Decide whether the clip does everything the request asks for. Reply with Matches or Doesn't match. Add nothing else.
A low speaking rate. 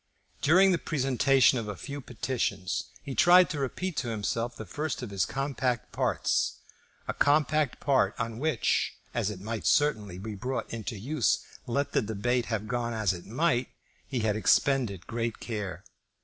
Doesn't match